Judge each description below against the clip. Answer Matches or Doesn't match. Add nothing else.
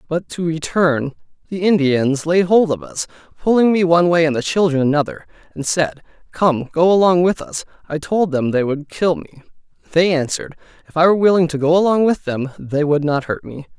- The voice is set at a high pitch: Doesn't match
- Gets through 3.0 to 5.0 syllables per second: Doesn't match